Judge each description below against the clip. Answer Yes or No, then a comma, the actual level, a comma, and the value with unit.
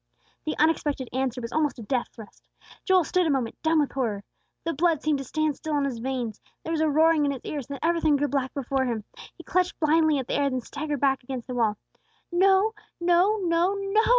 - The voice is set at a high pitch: Yes, very high, 290 Hz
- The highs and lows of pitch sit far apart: No, average, 4.0 semitones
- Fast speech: Yes, fast, 225 wpm